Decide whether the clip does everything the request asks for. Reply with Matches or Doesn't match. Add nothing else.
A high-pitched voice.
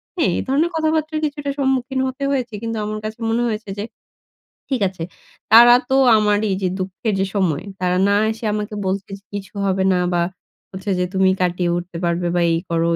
Matches